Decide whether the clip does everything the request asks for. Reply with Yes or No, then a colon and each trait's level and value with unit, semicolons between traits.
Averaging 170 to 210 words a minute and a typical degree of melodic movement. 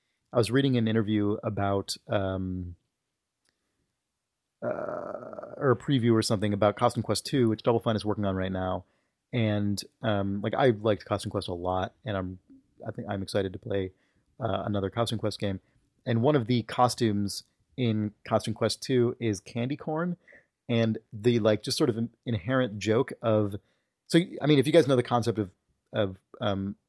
Yes: average, 180 wpm; average, 3.1 semitones